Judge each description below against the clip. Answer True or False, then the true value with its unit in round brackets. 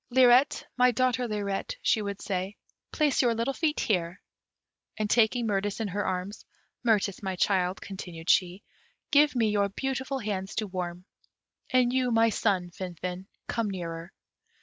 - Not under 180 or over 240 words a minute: False (150 wpm)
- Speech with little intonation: False (4.6 semitones)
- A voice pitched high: True (205 Hz)